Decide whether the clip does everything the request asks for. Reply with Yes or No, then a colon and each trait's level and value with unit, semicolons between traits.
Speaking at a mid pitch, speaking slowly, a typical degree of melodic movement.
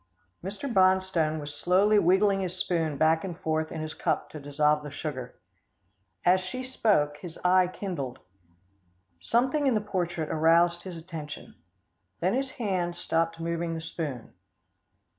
No: medium, 170 Hz; average, 145 wpm; average, 3.3 semitones